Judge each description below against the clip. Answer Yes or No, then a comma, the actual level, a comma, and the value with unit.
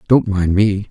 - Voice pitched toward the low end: Yes, low, 100 Hz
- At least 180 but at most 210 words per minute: Yes, average, 200 wpm